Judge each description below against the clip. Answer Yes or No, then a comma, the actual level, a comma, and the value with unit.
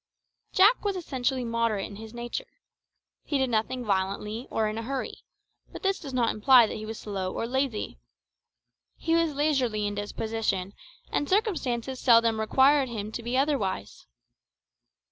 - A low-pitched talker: No, high, 235 Hz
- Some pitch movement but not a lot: Yes, average, 4.1 semitones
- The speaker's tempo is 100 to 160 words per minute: Yes, average, 155 wpm